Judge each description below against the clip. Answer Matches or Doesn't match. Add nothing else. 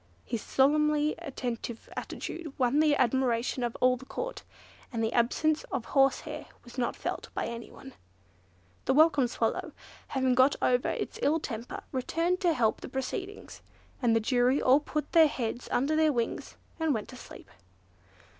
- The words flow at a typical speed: Matches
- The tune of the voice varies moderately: Matches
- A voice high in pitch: Matches